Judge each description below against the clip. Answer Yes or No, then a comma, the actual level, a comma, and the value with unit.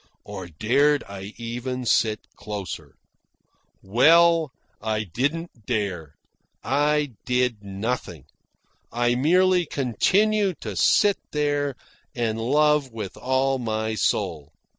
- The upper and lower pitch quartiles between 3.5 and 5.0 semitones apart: No, wide, 5.5 semitones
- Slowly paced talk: Yes, slow, 100 wpm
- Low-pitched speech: Yes, low, 125 Hz